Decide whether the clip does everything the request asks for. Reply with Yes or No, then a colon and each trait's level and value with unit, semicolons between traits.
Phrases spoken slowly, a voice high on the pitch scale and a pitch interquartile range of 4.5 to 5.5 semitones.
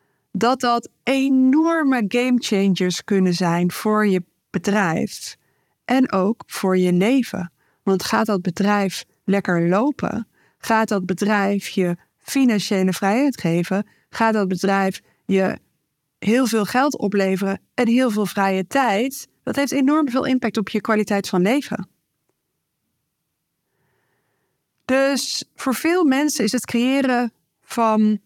Yes: slow, 125 wpm; high, 210 Hz; average, 4.8 semitones